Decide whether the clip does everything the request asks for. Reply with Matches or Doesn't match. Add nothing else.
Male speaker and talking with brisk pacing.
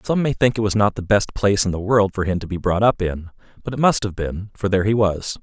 Matches